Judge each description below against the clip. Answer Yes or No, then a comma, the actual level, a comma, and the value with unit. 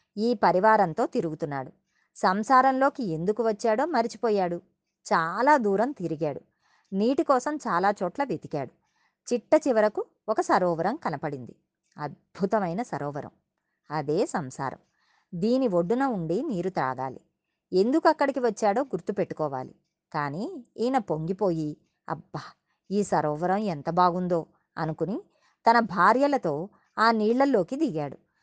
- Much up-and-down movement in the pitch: Yes, wide, 6.2 semitones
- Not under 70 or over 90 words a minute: No, average, 100 wpm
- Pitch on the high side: Yes, high, 205 Hz